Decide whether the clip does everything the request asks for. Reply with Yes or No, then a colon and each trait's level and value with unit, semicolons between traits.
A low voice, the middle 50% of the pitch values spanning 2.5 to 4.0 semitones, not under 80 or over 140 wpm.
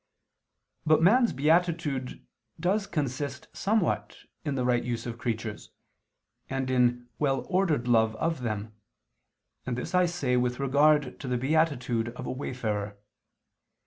No: low, 130 Hz; average, 4.5 semitones; slow, 135 wpm